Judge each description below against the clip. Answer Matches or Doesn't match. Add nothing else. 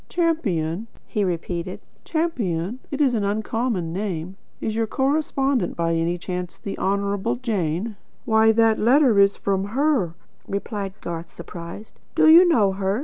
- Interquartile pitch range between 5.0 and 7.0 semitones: Matches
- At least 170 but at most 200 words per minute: Doesn't match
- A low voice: Doesn't match